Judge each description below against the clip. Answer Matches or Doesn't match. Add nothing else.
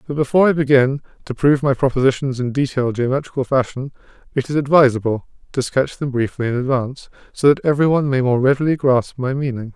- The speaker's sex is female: Doesn't match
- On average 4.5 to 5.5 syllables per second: Doesn't match